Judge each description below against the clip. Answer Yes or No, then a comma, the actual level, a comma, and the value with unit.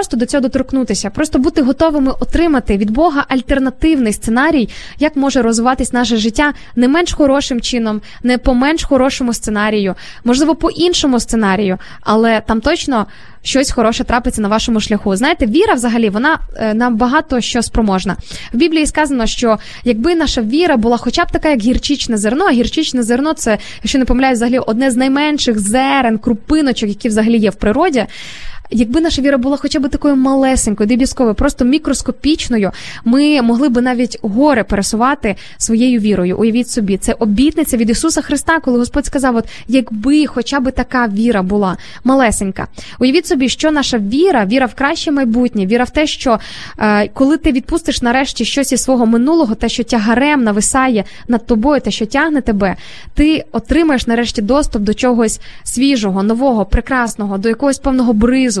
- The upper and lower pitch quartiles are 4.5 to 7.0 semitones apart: No, average, 3.7 semitones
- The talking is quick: Yes, fast, 165 wpm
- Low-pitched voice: No, very high, 250 Hz